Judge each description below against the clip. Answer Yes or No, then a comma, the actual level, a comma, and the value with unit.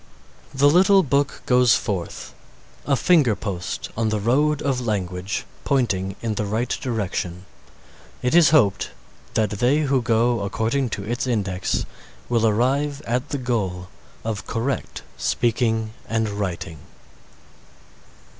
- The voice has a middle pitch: No, low, 115 Hz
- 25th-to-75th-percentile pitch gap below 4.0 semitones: No, average, 4.7 semitones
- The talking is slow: Yes, slow, 125 wpm